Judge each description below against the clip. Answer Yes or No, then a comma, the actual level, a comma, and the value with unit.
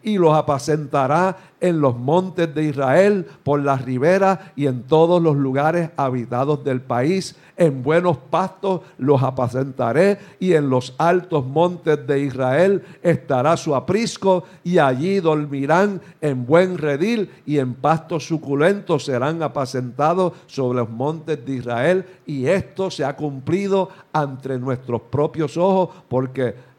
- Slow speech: No, average, 135 wpm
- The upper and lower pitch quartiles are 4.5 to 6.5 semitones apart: Yes, average, 4.9 semitones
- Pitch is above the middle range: No, medium, 155 Hz